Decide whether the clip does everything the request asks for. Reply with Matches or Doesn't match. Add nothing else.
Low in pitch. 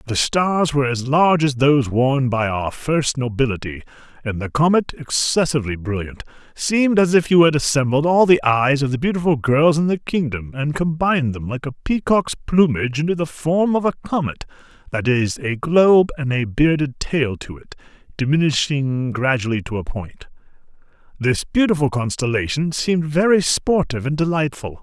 Doesn't match